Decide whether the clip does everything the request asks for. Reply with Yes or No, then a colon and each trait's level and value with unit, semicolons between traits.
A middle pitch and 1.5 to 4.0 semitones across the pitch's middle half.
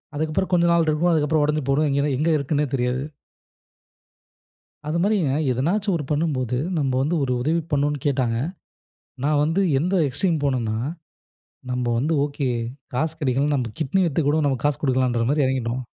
Yes: medium, 145 Hz; average, 3.3 semitones